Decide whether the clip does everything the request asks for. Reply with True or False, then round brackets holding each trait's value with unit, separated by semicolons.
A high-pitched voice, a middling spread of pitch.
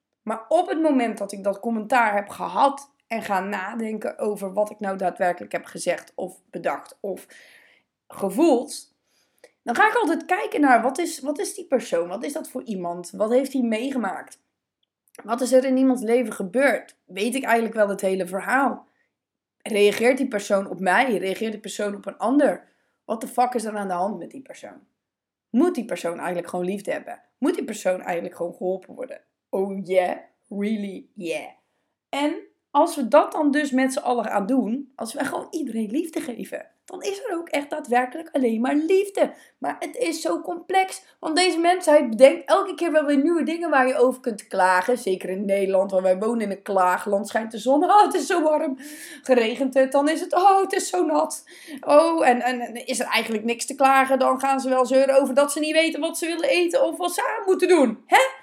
False (255 Hz; 6.7 semitones)